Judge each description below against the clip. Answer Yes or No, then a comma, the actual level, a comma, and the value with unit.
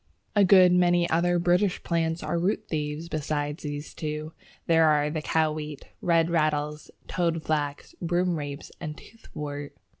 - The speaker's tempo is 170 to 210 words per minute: No, average, 140 wpm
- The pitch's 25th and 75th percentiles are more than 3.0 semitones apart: No, narrow, 2.5 semitones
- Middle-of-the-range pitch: Yes, medium, 160 Hz